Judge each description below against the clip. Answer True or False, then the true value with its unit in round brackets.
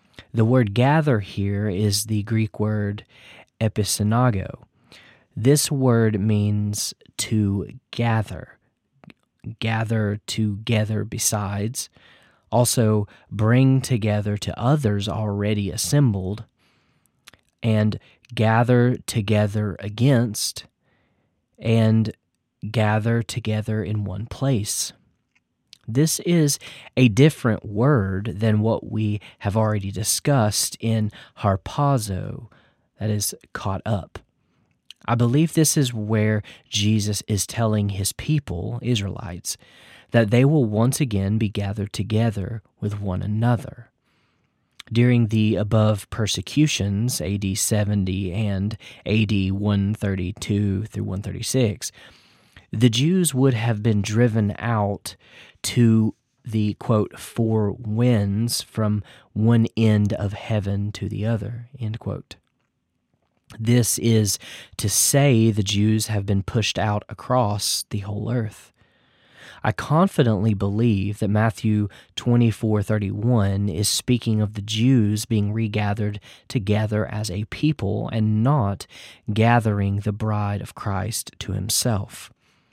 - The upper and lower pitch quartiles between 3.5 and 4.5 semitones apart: False (2.5 semitones)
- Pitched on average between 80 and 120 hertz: True (110 Hz)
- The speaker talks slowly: True (105 wpm)